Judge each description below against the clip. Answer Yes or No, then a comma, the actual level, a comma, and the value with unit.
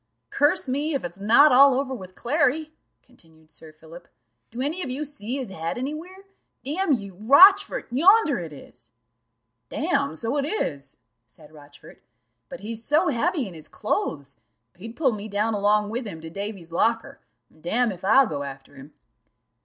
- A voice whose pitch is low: No, high, 225 Hz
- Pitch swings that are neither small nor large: No, wide, 9.0 semitones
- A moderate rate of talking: Yes, average, 170 wpm